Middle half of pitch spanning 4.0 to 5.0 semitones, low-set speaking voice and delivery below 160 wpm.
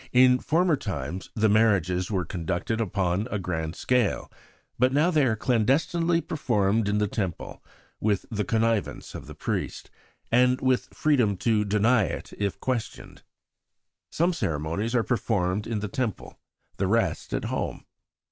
Yes: average, 4.6 semitones; low, 110 Hz; average, 145 wpm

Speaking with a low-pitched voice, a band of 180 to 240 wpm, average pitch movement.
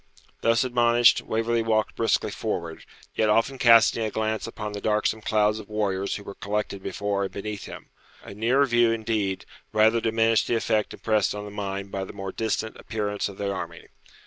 No: low, 110 Hz; average, 185 wpm; narrow, 1.9 semitones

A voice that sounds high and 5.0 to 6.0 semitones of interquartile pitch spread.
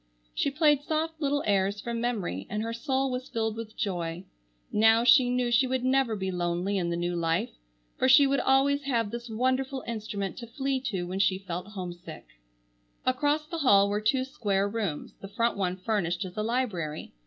Yes: high, 225 Hz; wide, 5.4 semitones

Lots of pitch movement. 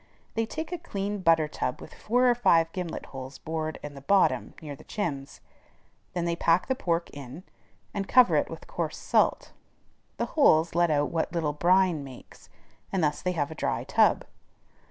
No: average, 4.6 semitones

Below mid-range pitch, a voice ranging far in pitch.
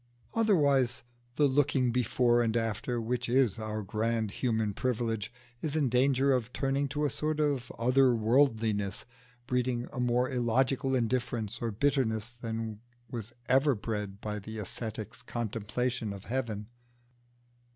No: low, 120 Hz; average, 3.0 semitones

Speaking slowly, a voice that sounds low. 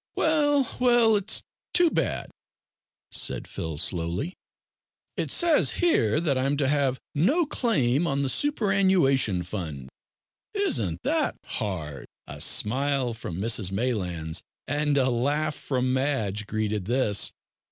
Yes: slow, 120 wpm; low, 130 Hz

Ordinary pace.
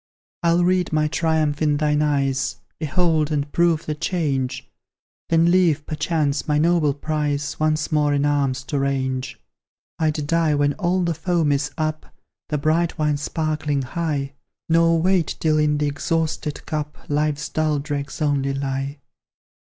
Yes: average, 150 wpm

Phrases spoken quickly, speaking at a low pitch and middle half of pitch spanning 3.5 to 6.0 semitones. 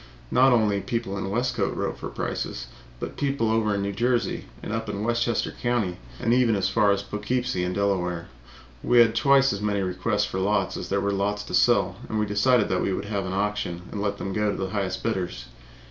No: fast, 225 wpm; low, 105 Hz; average, 2.9 semitones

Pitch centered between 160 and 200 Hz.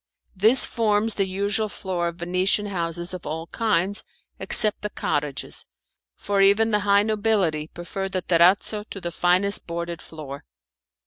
Yes: high, 190 Hz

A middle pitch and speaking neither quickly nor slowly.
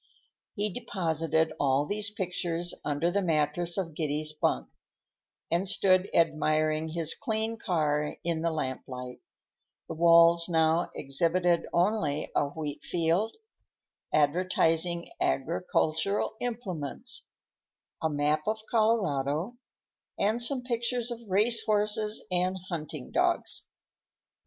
No: medium, 170 Hz; slow, 105 wpm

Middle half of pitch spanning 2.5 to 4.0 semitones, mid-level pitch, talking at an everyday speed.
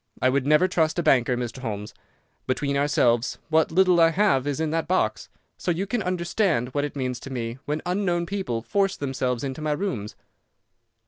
No: wide, 5.5 semitones; medium, 145 Hz; average, 190 wpm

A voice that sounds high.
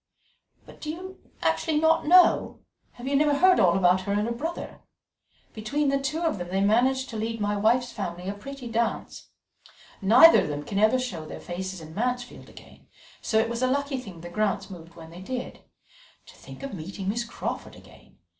Yes: high, 225 Hz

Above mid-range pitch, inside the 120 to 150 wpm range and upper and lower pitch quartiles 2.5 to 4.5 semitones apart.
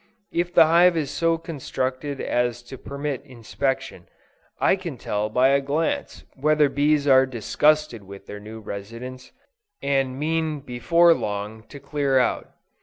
No: low, 135 Hz; average, 145 wpm; average, 3.9 semitones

